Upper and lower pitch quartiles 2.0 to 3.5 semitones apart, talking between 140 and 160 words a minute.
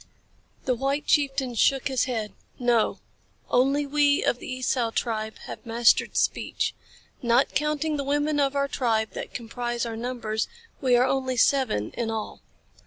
Yes: average, 3.1 semitones; average, 155 wpm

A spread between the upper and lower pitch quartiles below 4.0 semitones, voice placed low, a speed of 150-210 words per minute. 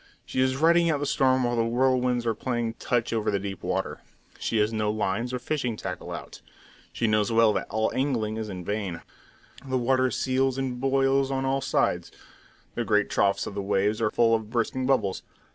Yes: average, 3.5 semitones; low, 120 Hz; average, 200 wpm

